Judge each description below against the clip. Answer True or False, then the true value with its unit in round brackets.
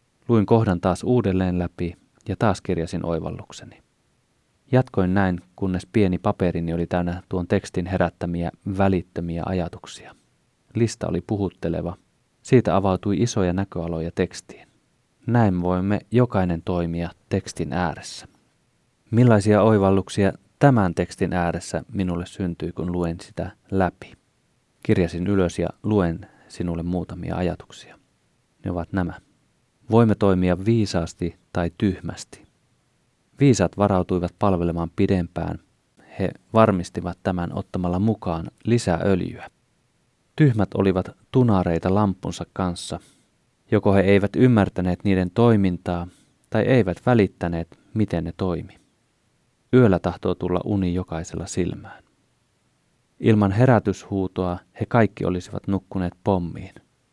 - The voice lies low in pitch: True (95 Hz)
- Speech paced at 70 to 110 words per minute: True (105 wpm)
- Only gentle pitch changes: False (3.0 semitones)